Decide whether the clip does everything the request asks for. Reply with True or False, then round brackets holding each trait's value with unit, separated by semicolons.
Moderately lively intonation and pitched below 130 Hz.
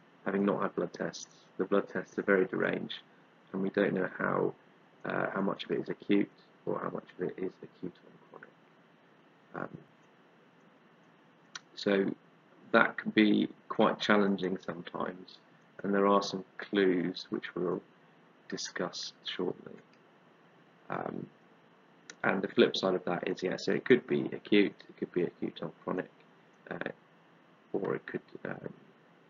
False (0.9 semitones; 100 Hz)